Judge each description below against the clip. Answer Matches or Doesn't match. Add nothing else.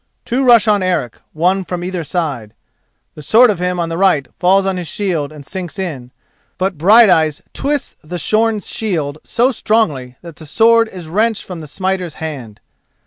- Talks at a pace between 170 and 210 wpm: Matches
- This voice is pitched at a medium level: Matches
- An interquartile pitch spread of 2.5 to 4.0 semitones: Doesn't match